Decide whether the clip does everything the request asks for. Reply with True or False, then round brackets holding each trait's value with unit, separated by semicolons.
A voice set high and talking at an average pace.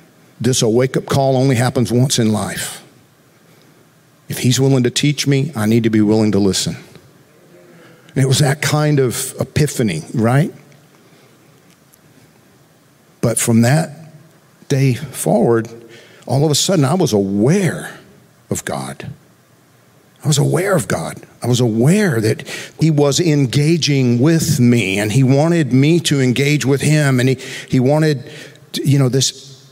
False (140 Hz; 150 wpm)